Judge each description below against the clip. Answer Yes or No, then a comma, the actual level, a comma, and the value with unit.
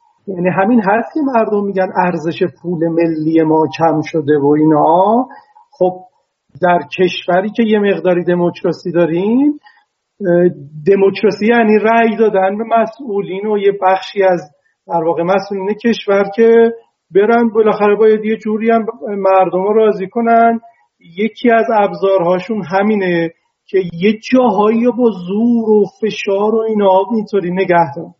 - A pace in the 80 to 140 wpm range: Yes, average, 130 wpm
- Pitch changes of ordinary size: Yes, average, 3.7 semitones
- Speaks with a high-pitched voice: Yes, high, 200 Hz